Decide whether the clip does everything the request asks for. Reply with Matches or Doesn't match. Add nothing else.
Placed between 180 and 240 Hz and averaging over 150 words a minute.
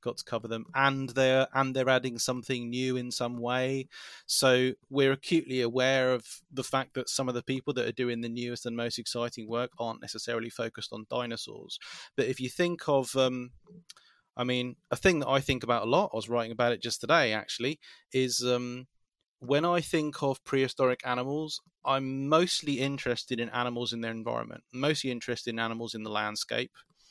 Doesn't match